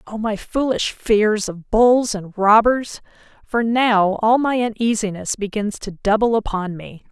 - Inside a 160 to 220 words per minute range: No, average, 145 wpm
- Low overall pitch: No, high, 215 Hz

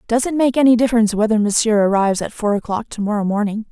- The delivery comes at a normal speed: No, fast, 225 wpm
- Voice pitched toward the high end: Yes, high, 220 Hz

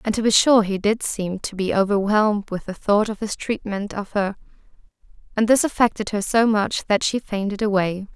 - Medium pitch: No, high, 205 Hz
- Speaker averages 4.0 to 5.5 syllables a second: Yes, 5.1 syllables/s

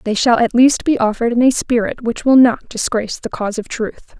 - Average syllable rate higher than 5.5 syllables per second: Yes, 5.7 syllables/s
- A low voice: No, high, 235 Hz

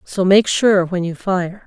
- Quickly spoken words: Yes, fast, 215 wpm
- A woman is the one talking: Yes, female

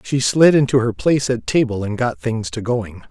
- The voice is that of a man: Yes, male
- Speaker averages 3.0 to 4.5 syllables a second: No, 5.1 syllables/s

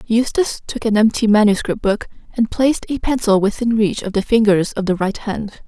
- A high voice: Yes, high, 220 Hz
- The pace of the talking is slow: No, average, 200 wpm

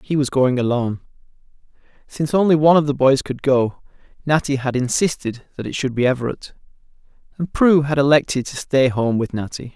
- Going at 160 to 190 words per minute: Yes, average, 180 wpm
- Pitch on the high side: No, low, 135 Hz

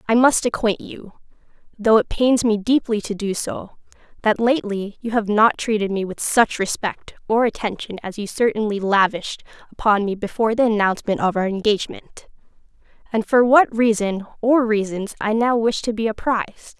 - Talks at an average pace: Yes, average, 170 wpm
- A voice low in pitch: No, high, 220 Hz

